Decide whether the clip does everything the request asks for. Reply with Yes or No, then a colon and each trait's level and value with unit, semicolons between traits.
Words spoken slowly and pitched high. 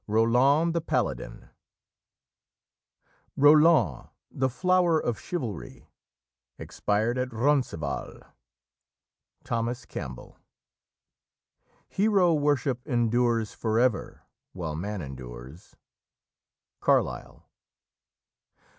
No: slow, 70 wpm; low, 120 Hz